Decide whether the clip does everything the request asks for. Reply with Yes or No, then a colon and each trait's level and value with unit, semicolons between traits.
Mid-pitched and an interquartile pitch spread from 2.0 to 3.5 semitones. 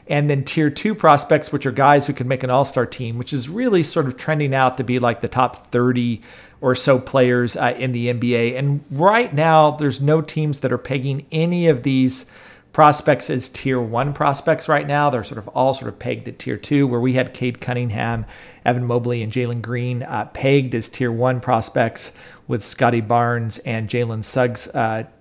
No: low, 130 Hz; average, 3.0 semitones